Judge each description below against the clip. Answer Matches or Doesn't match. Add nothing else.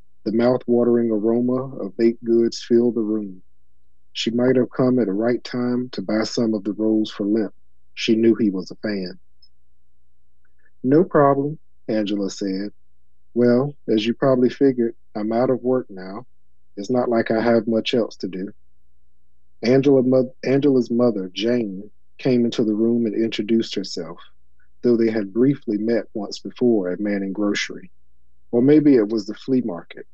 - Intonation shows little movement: Doesn't match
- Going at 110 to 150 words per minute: Doesn't match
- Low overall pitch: Matches